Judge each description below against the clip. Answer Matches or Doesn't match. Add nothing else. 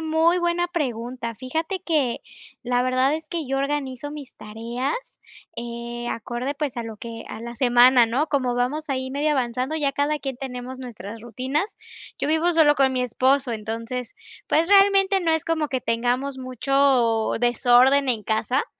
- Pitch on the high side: Matches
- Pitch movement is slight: Doesn't match